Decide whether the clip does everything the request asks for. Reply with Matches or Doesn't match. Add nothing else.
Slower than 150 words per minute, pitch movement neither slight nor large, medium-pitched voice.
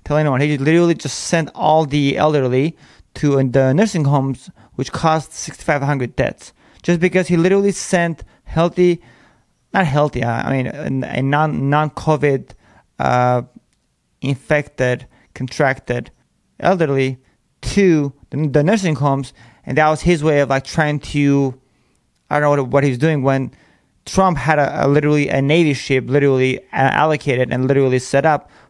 Matches